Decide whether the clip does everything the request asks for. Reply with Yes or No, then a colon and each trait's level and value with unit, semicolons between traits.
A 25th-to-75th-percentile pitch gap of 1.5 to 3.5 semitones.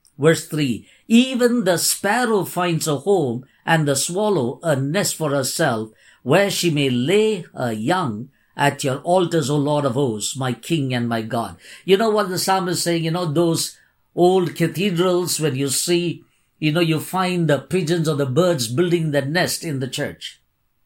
No: average, 4.3 semitones